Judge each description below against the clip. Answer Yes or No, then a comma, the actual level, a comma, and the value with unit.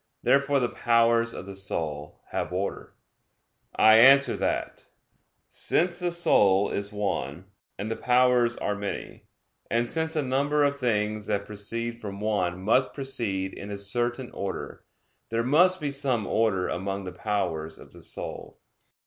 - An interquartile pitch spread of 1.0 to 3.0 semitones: No, average, 4.8 semitones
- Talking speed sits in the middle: Yes, average, 150 wpm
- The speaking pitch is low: Yes, low, 115 Hz